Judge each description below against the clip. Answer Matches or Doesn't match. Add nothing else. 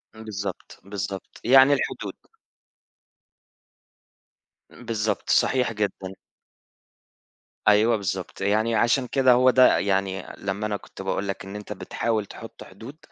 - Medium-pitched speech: Doesn't match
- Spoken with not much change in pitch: Doesn't match